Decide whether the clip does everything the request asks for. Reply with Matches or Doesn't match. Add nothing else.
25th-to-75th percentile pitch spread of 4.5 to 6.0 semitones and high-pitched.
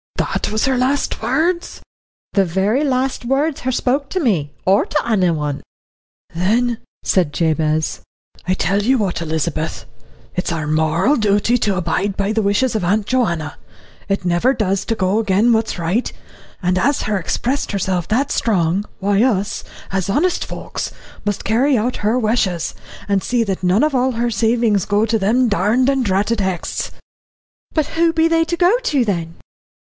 Matches